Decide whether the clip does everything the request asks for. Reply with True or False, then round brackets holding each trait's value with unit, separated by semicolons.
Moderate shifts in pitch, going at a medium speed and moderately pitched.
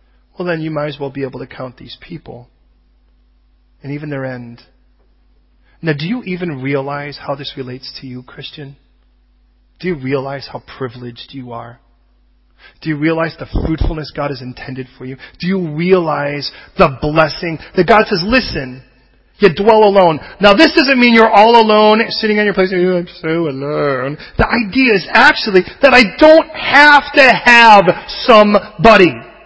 False (8.1 semitones; 170 wpm; 150 Hz)